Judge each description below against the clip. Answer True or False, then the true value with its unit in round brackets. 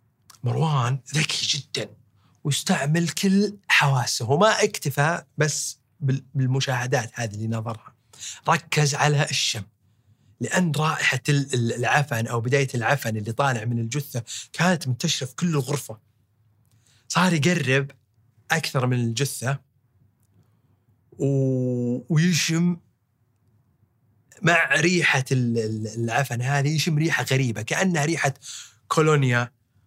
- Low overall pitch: True (130 Hz)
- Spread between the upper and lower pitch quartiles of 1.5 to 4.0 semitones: False (4.4 semitones)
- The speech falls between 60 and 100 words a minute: True (95 wpm)